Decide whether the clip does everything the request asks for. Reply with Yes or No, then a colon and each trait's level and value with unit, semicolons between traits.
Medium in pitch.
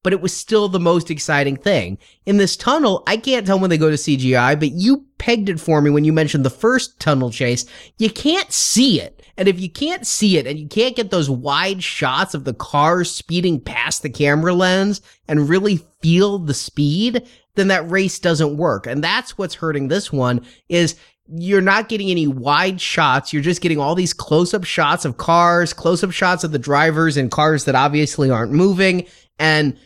Yes: medium, 170 Hz